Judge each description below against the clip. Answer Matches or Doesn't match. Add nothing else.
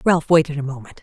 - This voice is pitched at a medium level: Matches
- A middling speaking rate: Doesn't match